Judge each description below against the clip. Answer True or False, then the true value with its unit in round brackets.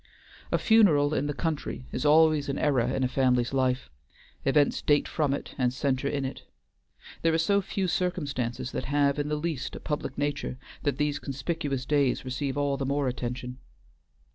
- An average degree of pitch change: False (2.3 semitones)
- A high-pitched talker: False (140 Hz)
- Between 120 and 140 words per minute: False (180 wpm)